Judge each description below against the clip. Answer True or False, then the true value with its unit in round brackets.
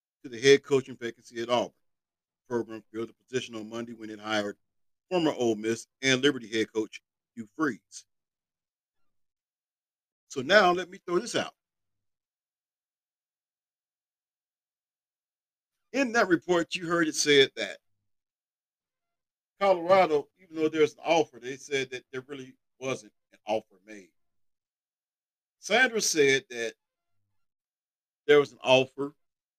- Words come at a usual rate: False (130 wpm)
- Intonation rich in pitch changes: True (6.6 semitones)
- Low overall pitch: True (130 Hz)